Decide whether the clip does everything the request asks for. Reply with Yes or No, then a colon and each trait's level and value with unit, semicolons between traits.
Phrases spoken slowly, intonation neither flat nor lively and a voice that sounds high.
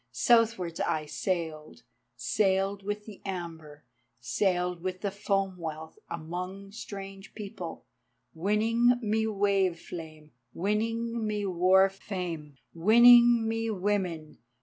Yes: slow, 105 wpm; average, 3.9 semitones; high, 195 Hz